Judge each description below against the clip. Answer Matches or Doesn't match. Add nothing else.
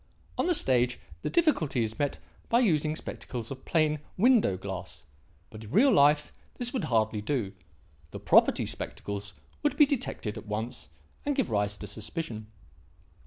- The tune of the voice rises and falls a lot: Matches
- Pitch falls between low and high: Doesn't match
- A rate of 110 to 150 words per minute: Doesn't match